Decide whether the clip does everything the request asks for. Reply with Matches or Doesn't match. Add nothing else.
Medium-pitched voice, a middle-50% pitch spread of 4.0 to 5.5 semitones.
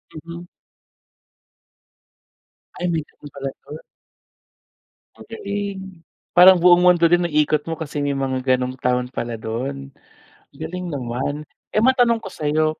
Matches